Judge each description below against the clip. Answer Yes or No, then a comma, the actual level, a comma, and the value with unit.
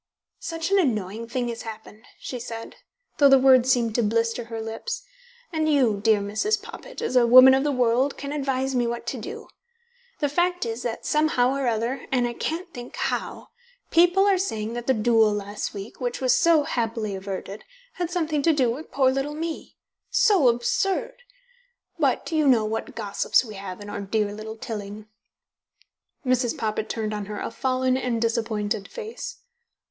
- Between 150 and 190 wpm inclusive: Yes, average, 180 wpm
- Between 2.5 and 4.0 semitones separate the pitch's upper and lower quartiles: No, average, 5.0 semitones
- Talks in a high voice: Yes, high, 245 Hz